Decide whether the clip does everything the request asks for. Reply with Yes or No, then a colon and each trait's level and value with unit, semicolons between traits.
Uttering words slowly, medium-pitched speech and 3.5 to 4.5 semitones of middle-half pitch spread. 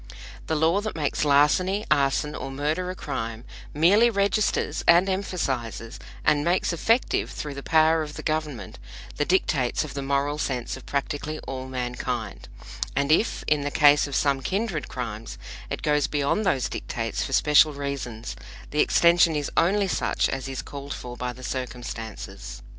No: average, 165 wpm; medium, 145 Hz; average, 3.8 semitones